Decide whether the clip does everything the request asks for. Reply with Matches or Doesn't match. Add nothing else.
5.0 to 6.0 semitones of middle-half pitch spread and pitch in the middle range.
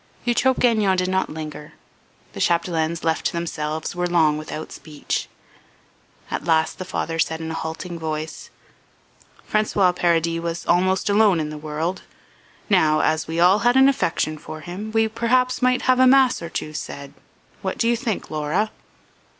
Matches